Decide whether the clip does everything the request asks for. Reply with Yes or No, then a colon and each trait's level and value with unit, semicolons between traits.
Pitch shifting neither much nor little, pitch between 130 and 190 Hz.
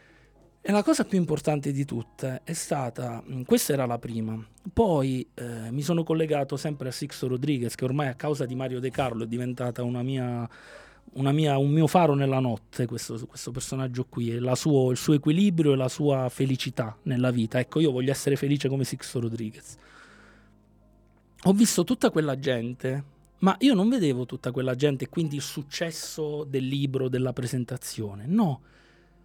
Yes: average, 3.4 semitones; low, 135 Hz